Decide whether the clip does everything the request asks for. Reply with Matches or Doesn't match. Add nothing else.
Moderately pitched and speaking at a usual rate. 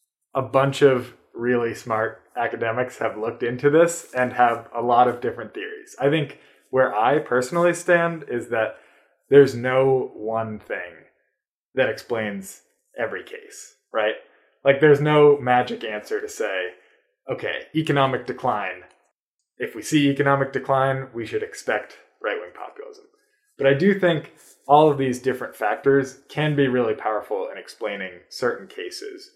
Matches